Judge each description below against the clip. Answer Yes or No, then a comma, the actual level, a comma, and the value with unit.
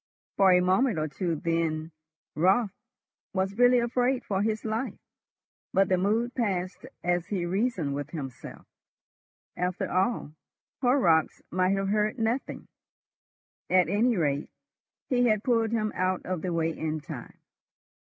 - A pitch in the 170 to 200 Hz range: Yes, high, 190 Hz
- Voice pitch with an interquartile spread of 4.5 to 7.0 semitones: Yes, average, 4.8 semitones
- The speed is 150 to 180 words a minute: No, average, 140 wpm